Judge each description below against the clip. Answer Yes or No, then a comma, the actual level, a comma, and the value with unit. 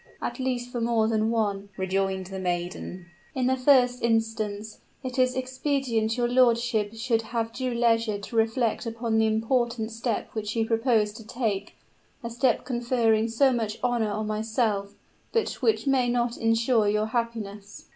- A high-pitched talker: Yes, high, 225 Hz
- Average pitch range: No, narrow, 2.2 semitones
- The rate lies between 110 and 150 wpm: No, average, 160 wpm